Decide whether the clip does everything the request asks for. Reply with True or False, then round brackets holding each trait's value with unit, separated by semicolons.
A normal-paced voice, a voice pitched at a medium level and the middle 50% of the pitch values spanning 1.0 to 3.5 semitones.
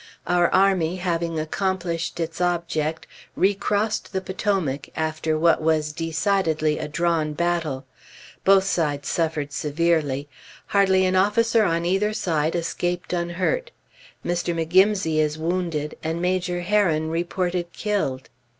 False (120 wpm; 170 Hz; 2.9 semitones)